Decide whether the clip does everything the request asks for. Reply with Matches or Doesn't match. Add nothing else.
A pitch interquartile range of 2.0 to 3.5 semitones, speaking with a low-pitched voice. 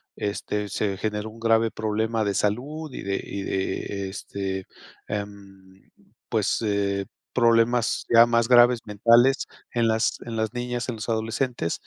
Matches